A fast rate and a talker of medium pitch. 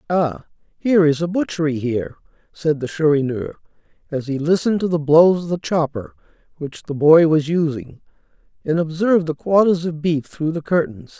No: average, 170 wpm; medium, 160 Hz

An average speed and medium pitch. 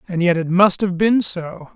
No: fast, 240 wpm; medium, 180 Hz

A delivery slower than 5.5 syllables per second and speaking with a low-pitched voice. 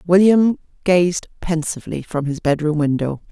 No: 4.7 syllables/s; medium, 165 Hz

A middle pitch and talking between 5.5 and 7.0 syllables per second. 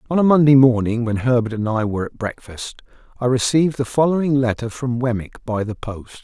No: low, 125 Hz; 5.7 syllables/s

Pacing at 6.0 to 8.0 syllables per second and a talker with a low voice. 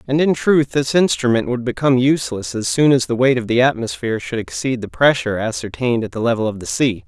Yes: 6.2 syllables/s; low, 120 Hz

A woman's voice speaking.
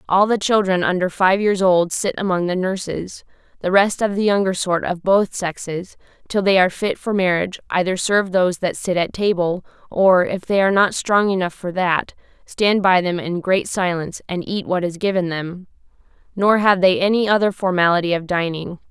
Yes: female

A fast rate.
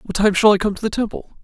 Yes: fast, 335 wpm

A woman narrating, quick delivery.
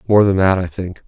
No: male; fast, 280 wpm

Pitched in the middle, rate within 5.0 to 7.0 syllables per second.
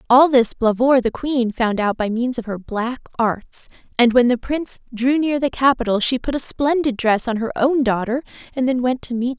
No: high, 245 Hz; 5.1 syllables/s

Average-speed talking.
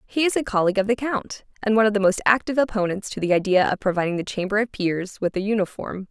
No: fast, 255 wpm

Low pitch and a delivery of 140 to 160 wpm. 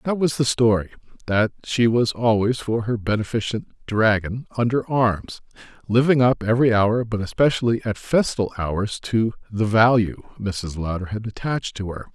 Yes: low, 110 Hz; average, 155 wpm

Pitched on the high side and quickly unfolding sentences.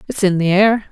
Yes: high, 200 Hz; fast, 260 wpm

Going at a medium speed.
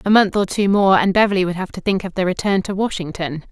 No: fast, 275 wpm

